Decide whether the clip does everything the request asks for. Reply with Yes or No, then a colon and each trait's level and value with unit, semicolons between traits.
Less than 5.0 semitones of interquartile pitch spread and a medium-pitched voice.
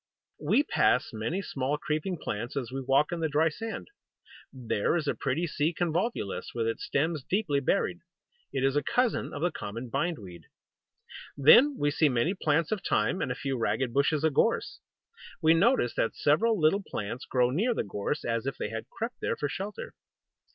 No: wide, 5.6 semitones; medium, 145 Hz